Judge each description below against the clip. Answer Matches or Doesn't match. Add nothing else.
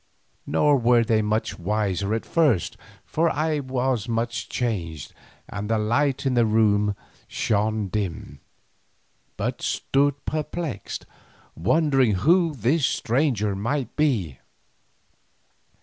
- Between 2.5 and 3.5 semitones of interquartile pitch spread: Doesn't match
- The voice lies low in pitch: Matches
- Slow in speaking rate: Matches